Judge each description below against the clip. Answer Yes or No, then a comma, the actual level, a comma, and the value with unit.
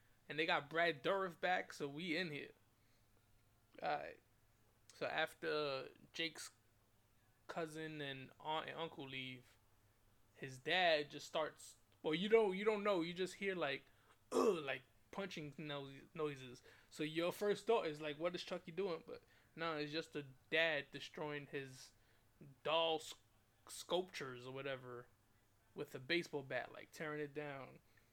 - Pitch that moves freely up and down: Yes, wide, 5.7 semitones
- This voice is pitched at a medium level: Yes, medium, 145 Hz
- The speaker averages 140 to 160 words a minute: Yes, average, 150 wpm